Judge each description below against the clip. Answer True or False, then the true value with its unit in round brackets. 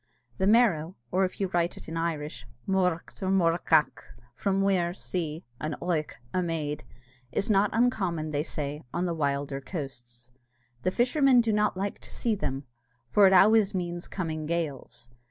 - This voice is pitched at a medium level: True (175 Hz)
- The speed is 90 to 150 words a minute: False (170 wpm)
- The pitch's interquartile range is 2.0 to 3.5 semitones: False (4.2 semitones)